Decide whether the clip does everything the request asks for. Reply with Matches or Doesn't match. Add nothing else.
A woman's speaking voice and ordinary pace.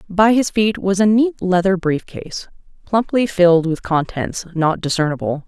Matches